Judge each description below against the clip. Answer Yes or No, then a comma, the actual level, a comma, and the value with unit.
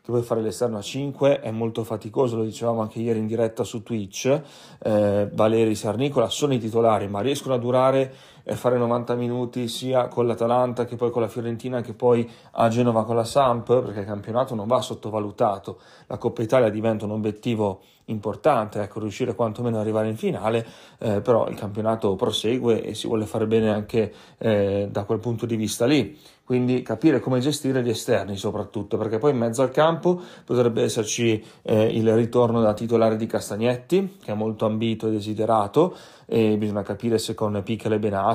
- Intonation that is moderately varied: No, narrow, 2.1 semitones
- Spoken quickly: Yes, fast, 190 wpm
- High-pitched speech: No, low, 115 Hz